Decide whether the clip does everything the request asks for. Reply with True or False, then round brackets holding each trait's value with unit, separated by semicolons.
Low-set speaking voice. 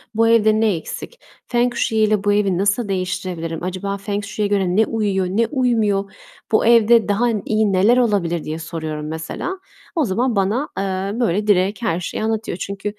False (205 Hz)